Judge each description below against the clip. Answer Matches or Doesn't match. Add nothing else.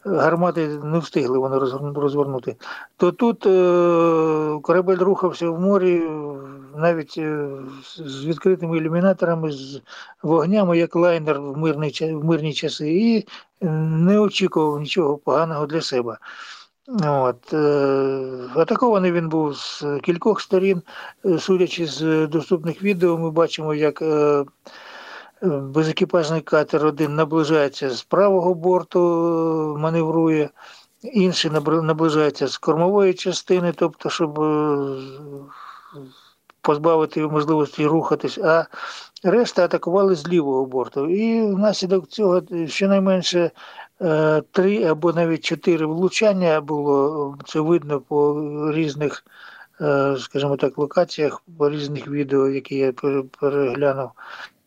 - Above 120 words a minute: Doesn't match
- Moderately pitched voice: Matches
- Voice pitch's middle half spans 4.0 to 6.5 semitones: Doesn't match